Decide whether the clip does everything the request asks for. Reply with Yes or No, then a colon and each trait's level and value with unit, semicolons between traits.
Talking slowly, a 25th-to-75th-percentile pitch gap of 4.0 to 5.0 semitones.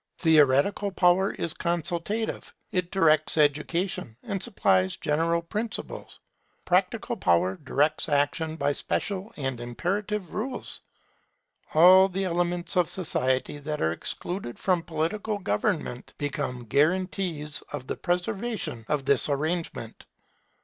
Yes: slow, 115 wpm; average, 4.6 semitones